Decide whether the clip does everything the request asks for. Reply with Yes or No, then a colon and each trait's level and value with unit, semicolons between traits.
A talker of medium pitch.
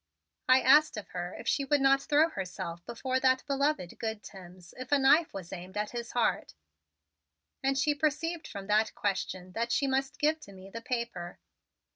No: high, 245 Hz